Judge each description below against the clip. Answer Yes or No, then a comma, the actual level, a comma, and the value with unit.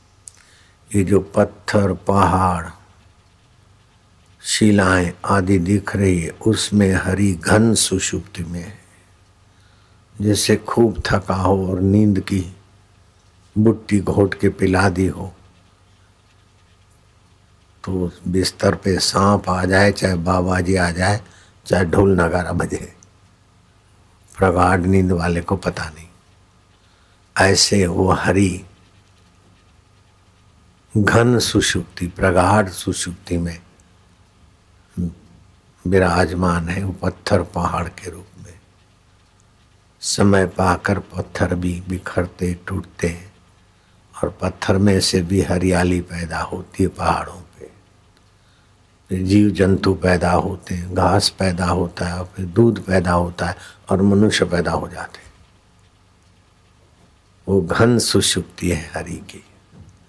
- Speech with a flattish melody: Yes, narrow, 1.8 semitones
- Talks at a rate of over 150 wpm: No, slow, 110 wpm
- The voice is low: Yes, very low, 95 Hz